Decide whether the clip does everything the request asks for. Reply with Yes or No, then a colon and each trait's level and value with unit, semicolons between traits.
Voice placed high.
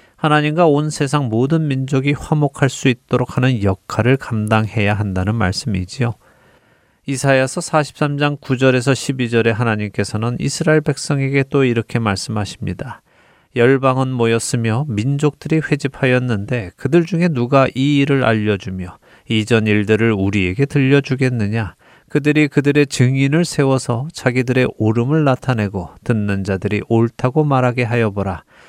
No: low, 125 Hz